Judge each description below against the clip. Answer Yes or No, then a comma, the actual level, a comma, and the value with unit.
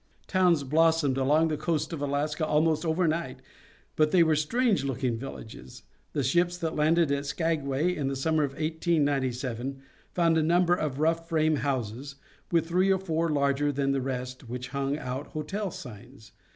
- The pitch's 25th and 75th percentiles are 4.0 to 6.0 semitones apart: No, average, 3.3 semitones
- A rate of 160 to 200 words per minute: Yes, average, 170 wpm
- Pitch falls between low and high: Yes, medium, 150 Hz